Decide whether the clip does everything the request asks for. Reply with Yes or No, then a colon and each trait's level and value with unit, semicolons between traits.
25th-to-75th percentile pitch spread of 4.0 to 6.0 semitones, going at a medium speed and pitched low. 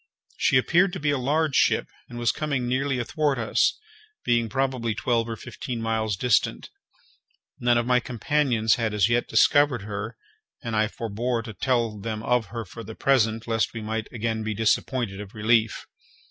No: narrow, 2.6 semitones; average, 175 wpm; low, 115 Hz